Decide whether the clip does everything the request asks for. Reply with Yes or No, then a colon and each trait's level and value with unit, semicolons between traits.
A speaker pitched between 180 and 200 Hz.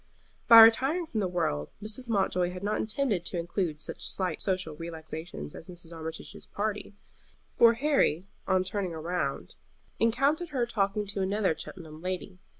Yes: high, 190 Hz